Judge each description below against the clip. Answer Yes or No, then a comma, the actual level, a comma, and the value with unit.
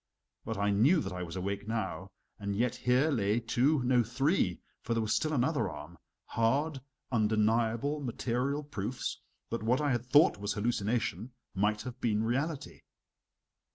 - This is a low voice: Yes, low, 115 Hz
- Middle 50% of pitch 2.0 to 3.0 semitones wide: No, average, 4.0 semitones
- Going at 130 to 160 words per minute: Yes, average, 155 wpm